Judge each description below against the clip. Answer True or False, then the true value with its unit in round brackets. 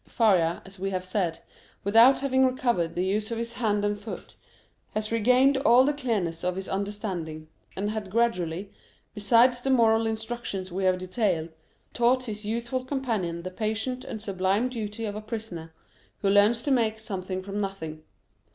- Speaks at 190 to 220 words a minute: False (170 wpm)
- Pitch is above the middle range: True (210 Hz)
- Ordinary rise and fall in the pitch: True (3.9 semitones)